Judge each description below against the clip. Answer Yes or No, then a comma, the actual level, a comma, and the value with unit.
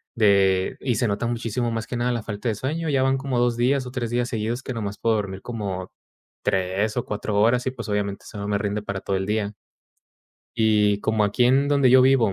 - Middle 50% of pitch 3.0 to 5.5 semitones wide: Yes, average, 3.4 semitones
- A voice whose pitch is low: Yes, low, 110 Hz